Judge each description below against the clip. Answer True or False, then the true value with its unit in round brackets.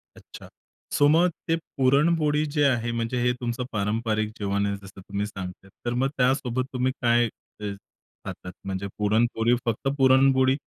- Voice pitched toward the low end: True (120 Hz)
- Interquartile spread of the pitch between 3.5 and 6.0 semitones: True (4.0 semitones)